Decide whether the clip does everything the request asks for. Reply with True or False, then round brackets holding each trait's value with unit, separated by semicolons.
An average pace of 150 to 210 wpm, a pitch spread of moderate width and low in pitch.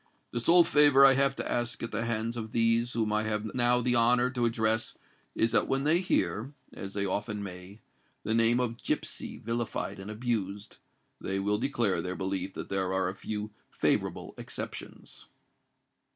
True (170 wpm; 3.1 semitones; 115 Hz)